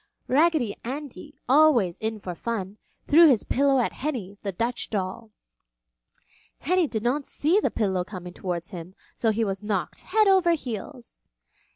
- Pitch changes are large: Yes, wide, 7.0 semitones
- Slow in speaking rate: No, average, 155 wpm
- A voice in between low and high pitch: No, high, 235 Hz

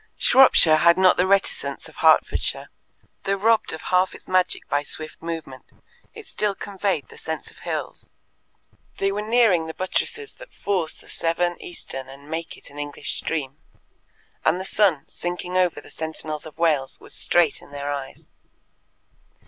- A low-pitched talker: No, medium, 170 Hz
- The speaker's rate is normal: Yes, average, 165 wpm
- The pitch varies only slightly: No, average, 3.9 semitones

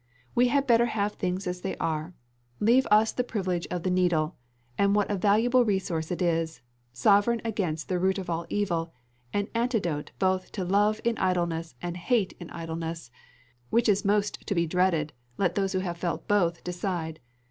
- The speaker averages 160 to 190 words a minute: Yes, average, 180 wpm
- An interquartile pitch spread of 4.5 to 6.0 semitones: No, average, 3.4 semitones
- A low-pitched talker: No, medium, 185 Hz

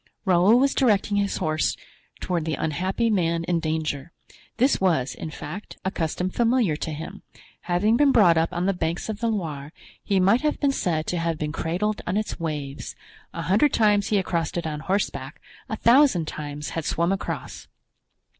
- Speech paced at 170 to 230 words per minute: Yes, average, 185 wpm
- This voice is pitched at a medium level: Yes, medium, 180 Hz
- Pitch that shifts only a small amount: No, average, 4.7 semitones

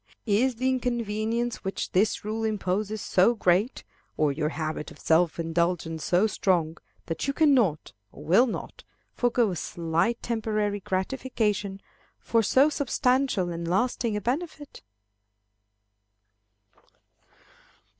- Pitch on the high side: Yes, high, 210 Hz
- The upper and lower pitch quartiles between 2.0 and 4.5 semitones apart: No, wide, 5.4 semitones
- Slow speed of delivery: Yes, slow, 115 wpm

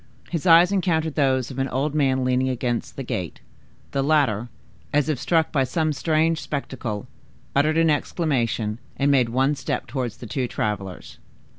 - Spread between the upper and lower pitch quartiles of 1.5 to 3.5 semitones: No, average, 4.0 semitones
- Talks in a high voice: No, low, 135 Hz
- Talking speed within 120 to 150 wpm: No, average, 165 wpm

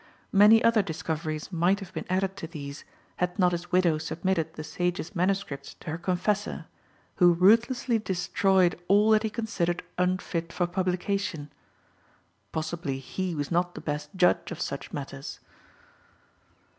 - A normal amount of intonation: Yes, average, 3.2 semitones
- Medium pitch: Yes, medium, 180 Hz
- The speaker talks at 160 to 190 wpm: No, average, 145 wpm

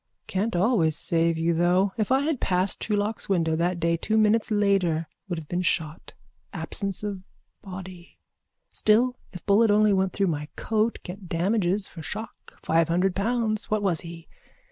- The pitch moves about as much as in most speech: Yes, average, 3.9 semitones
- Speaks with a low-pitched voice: No, high, 190 Hz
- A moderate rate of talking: Yes, average, 165 wpm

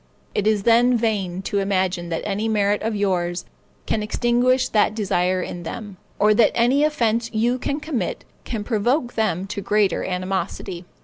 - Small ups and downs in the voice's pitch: No, average, 3.7 semitones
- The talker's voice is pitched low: No, high, 210 Hz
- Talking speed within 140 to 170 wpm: Yes, average, 165 wpm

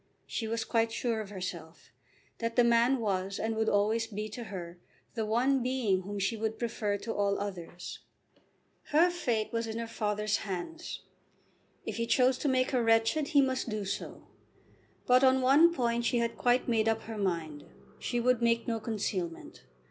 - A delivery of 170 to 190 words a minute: Yes, average, 180 wpm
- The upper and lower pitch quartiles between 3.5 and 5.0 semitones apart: No, average, 3.1 semitones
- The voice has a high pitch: Yes, high, 225 Hz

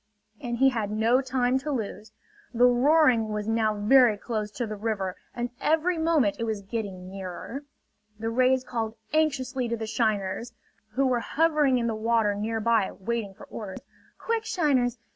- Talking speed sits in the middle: Yes, average, 165 wpm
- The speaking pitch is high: Yes, high, 235 Hz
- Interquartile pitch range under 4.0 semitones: Yes, average, 3.5 semitones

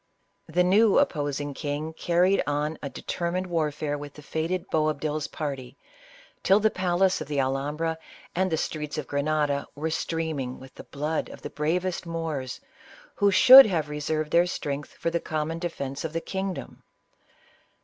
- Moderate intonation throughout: Yes, average, 3.1 semitones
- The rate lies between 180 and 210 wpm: No, average, 165 wpm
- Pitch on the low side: No, medium, 155 Hz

